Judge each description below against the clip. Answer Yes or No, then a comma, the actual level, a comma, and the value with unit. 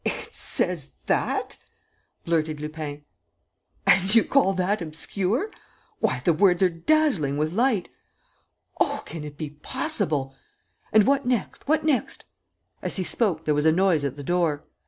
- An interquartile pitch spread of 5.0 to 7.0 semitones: Yes, average, 5.3 semitones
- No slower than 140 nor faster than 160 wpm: Yes, average, 155 wpm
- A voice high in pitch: No, medium, 170 Hz